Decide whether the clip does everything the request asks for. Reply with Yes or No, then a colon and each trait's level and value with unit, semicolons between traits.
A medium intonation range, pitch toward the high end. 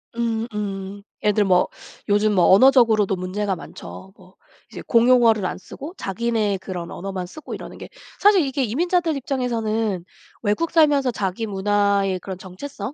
Yes: average, 4.3 semitones; high, 210 Hz